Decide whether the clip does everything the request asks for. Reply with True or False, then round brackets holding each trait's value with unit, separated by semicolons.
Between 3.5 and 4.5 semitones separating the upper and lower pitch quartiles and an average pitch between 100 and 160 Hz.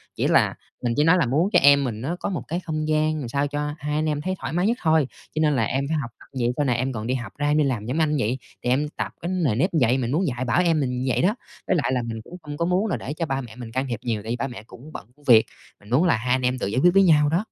True (4.2 semitones; 140 Hz)